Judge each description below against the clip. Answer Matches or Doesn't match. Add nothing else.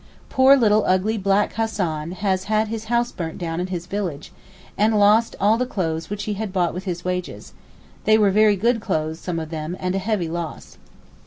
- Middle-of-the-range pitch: Doesn't match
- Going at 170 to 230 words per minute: Matches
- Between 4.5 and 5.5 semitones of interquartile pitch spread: Doesn't match